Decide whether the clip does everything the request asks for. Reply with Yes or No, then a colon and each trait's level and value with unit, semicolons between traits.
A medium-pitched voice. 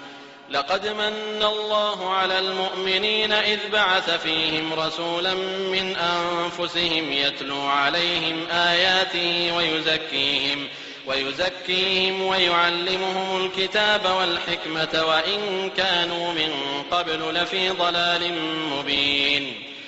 Yes: medium, 175 Hz